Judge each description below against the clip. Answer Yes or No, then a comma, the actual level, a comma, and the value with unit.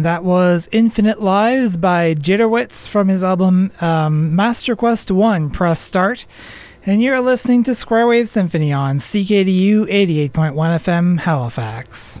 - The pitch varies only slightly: No, average, 5.0 semitones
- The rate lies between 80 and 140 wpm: Yes, slow, 135 wpm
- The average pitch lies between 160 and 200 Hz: Yes, high, 190 Hz